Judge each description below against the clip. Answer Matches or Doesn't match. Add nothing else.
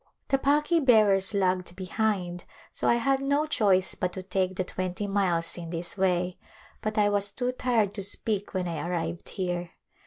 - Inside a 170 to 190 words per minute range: Matches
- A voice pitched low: Doesn't match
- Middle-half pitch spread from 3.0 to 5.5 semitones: Matches